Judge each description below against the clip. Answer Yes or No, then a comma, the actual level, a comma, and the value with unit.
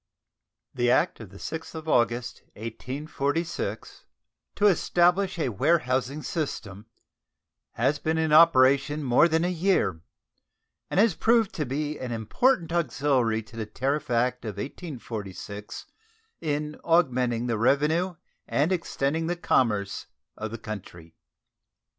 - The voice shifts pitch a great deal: Yes, wide, 5.8 semitones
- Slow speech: Yes, slow, 125 wpm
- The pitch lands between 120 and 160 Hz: Yes, medium, 140 Hz